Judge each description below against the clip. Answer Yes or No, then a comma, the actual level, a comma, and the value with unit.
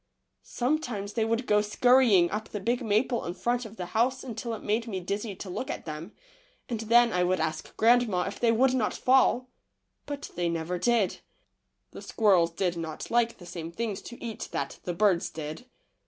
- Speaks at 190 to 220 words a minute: Yes, average, 195 wpm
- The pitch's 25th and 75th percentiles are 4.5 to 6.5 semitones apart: Yes, average, 5.1 semitones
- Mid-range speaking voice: No, high, 215 Hz